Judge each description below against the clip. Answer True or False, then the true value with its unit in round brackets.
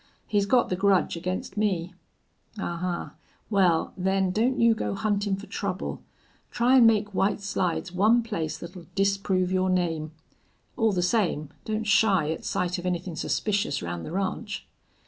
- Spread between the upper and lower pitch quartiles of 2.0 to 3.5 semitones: True (2.9 semitones)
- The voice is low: False (190 Hz)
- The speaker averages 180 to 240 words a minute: False (155 wpm)